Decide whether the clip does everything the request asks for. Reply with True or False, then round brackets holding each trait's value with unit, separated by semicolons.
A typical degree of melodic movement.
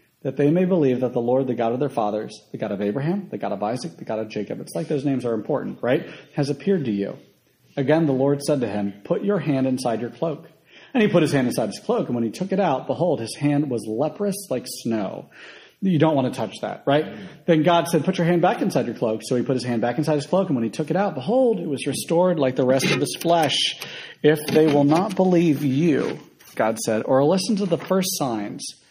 False (5.7 semitones)